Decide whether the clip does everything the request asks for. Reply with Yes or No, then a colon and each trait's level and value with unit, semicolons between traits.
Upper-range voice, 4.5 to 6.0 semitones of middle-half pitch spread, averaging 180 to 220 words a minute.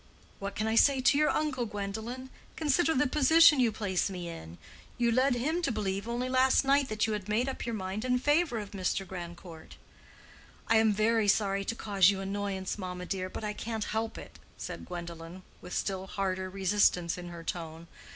Yes: high, 210 Hz; average, 4.9 semitones; average, 195 wpm